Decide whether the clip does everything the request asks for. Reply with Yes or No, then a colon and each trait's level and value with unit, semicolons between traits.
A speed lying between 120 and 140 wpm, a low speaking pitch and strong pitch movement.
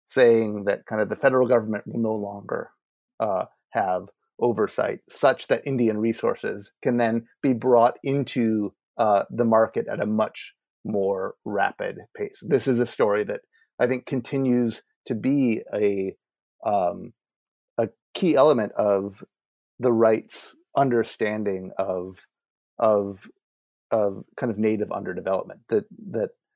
No: slow, 135 wpm; low, 115 Hz; average, 4.1 semitones